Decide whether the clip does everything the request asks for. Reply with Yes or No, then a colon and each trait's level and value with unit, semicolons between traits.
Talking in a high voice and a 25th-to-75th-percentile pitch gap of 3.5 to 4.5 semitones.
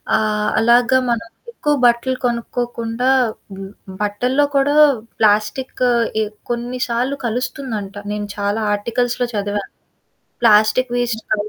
No: high, 235 Hz; average, 2.9 semitones